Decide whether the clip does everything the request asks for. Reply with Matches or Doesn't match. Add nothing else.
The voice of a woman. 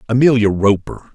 Doesn't match